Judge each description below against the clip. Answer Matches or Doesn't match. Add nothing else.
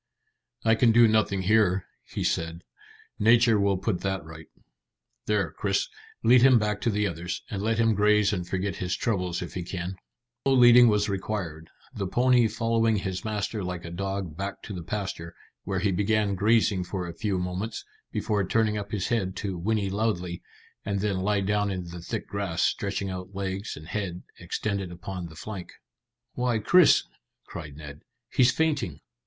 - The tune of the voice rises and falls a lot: Doesn't match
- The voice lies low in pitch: Matches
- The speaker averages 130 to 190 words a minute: Matches